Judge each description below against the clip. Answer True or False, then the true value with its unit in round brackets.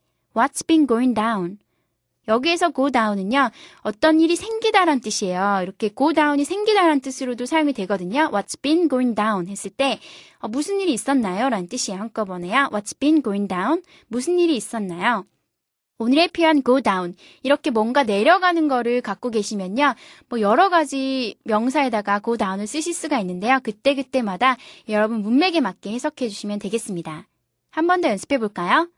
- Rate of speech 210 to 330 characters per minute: False (460 characters per minute)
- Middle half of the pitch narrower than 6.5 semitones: False (6.8 semitones)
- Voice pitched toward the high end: True (255 Hz)